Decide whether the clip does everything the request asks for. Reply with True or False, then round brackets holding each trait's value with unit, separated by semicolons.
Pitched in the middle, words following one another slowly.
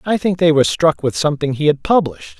False (165 Hz; 250 wpm)